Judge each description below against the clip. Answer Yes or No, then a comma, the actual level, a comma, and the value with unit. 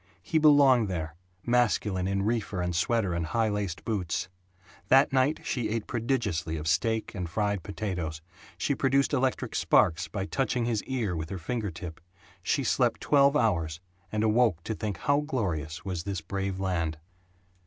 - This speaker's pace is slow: No, average, 165 wpm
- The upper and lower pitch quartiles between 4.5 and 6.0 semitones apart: Yes, wide, 5.6 semitones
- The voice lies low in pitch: Yes, low, 100 Hz